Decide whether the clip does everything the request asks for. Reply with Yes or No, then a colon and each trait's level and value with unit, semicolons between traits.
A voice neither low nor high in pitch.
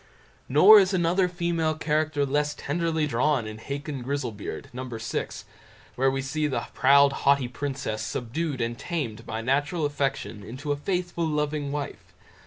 Yes: medium, 145 Hz